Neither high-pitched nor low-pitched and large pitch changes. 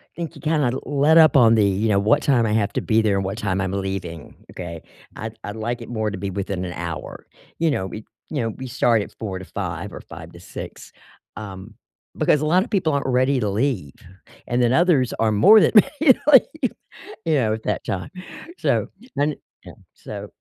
No: low, 110 Hz; wide, 6.4 semitones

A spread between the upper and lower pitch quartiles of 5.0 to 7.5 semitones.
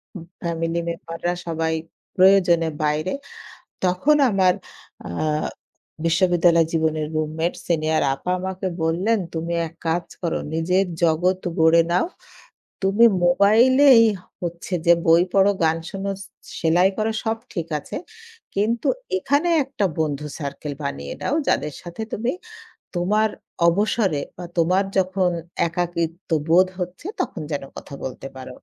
No: average, 3.2 semitones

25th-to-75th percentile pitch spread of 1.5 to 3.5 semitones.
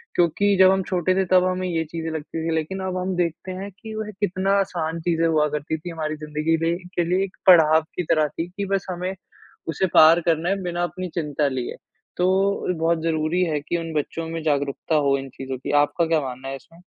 Yes: average, 2.8 semitones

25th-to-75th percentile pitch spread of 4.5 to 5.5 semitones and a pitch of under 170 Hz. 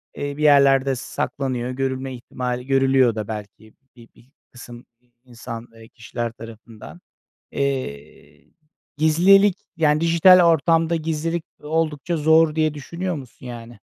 Yes: average, 4.9 semitones; low, 135 Hz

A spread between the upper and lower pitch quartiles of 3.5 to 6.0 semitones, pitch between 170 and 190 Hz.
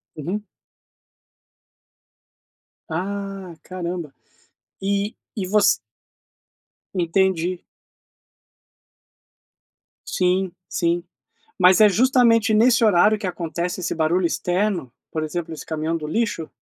No: average, 3.1 semitones; medium, 185 Hz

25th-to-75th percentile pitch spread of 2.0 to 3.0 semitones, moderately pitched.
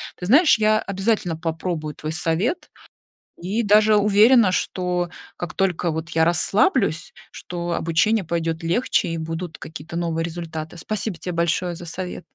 No: average, 3.8 semitones; medium, 175 Hz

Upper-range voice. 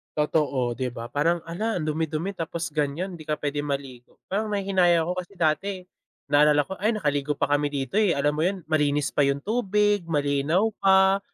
No: medium, 155 Hz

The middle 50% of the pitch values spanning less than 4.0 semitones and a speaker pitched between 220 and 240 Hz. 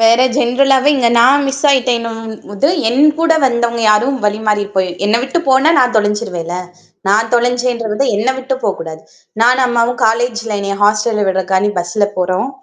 Yes: average, 3.4 semitones; high, 230 Hz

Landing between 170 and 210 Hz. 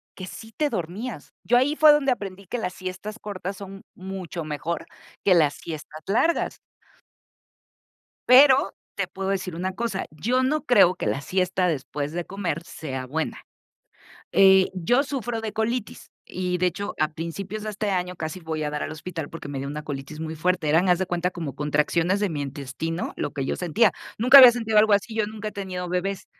Yes: medium, 185 Hz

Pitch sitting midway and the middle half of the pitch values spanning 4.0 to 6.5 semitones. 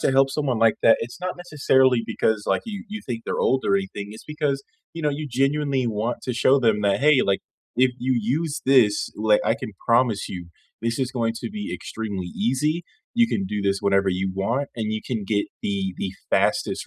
No: low, 120 Hz; average, 5.2 semitones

